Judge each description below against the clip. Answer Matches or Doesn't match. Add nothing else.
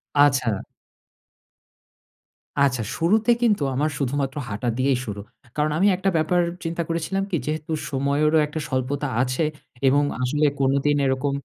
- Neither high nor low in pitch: Matches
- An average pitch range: Matches